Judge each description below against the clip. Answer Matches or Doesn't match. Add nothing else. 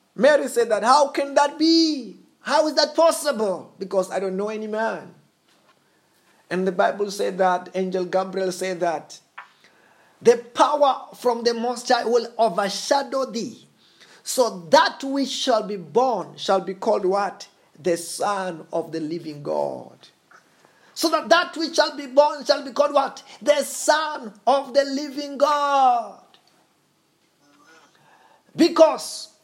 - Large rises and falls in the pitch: Matches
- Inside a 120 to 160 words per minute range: Matches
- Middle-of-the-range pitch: Doesn't match